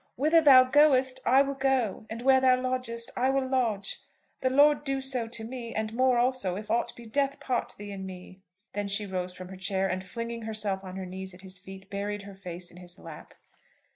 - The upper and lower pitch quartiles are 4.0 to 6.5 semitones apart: Yes, average, 5.2 semitones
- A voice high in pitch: Yes, high, 225 Hz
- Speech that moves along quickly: Yes, fast, 220 wpm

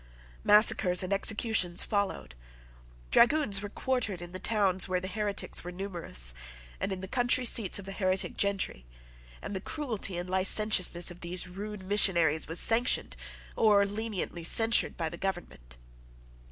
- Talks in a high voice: Yes, high, 195 Hz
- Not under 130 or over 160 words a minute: Yes, average, 150 wpm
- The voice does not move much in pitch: No, average, 3.0 semitones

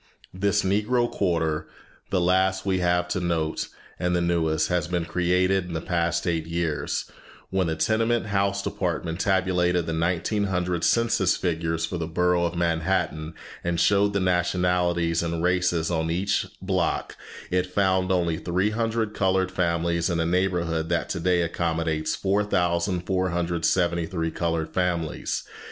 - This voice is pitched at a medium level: No, very low, 90 Hz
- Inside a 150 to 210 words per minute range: No, average, 140 wpm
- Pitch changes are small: Yes, narrow, 2.0 semitones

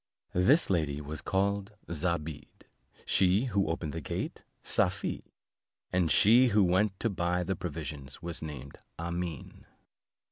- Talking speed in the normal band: No, slow, 130 wpm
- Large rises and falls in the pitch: No, average, 3.9 semitones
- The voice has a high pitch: No, very low, 85 Hz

